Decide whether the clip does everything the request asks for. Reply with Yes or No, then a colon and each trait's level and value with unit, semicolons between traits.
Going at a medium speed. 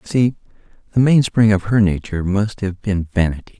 Yes: average, 185 wpm